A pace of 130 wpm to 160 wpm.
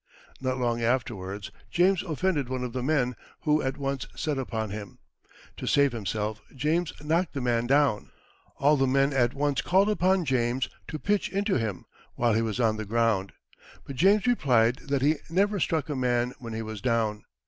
No: average, 185 wpm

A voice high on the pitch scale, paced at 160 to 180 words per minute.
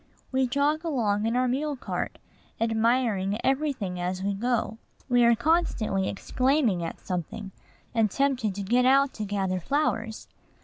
No: high, 230 Hz; average, 150 wpm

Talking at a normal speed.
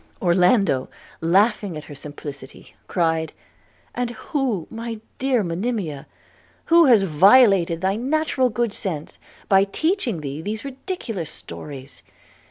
No: slow, 115 wpm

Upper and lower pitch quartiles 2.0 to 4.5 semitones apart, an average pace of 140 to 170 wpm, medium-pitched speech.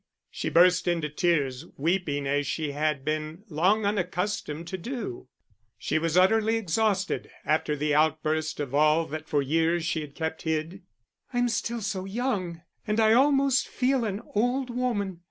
No: wide, 5.6 semitones; average, 155 wpm; medium, 170 Hz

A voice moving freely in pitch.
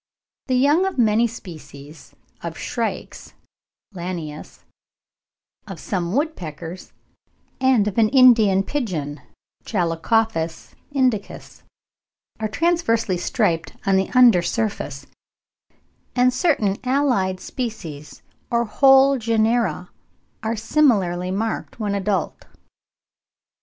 Yes: wide, 5.9 semitones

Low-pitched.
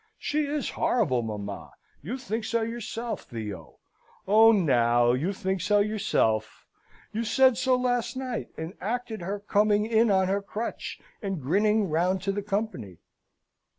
No: high, 205 Hz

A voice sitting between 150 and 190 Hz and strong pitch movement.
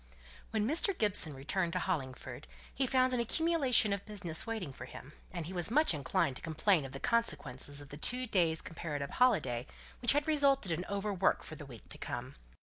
Yes: medium, 185 Hz; wide, 8.3 semitones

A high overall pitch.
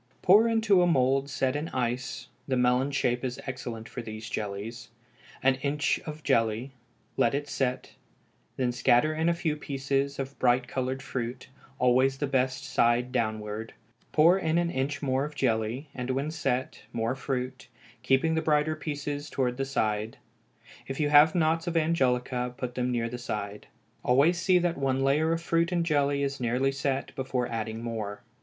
No: low, 135 Hz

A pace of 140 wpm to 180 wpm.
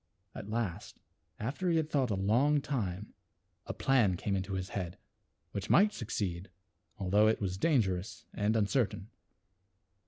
Yes: average, 145 wpm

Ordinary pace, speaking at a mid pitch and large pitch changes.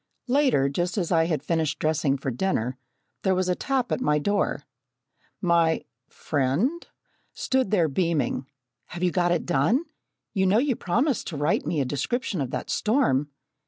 Yes: average, 170 wpm; medium, 175 Hz; wide, 6.5 semitones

